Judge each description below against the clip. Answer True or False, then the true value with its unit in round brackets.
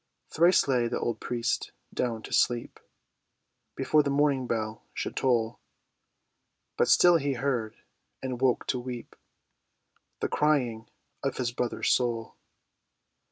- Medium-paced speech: False (120 wpm)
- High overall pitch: False (125 Hz)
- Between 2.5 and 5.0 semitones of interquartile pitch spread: True (2.8 semitones)